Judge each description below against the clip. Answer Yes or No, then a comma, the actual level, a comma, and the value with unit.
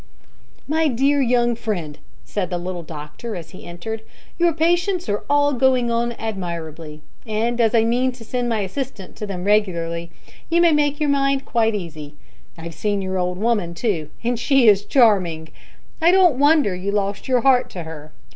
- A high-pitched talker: Yes, high, 220 Hz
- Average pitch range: No, wide, 6.7 semitones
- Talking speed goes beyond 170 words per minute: Yes, average, 180 wpm